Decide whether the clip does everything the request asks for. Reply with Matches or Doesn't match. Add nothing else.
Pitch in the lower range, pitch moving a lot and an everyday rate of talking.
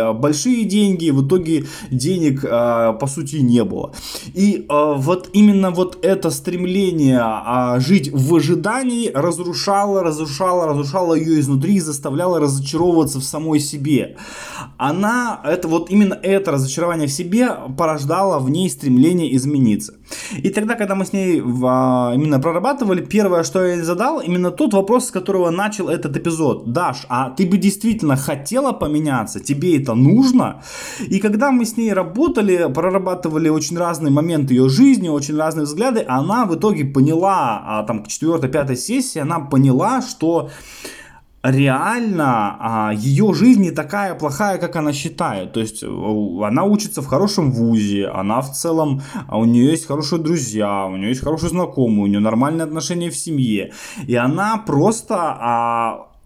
Doesn't match